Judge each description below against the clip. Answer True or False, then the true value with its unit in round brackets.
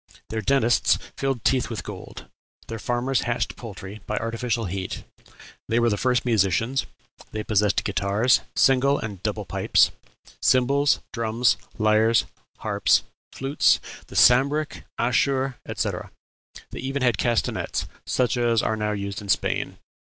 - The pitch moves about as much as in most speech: True (3.2 semitones)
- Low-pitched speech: True (115 Hz)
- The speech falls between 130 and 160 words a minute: True (135 wpm)